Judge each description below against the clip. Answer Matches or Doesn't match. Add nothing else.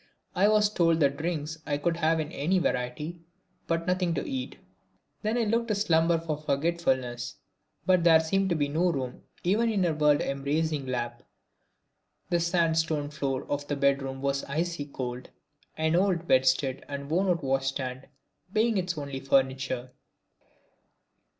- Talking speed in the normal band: Matches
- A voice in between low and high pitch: Matches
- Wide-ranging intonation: Doesn't match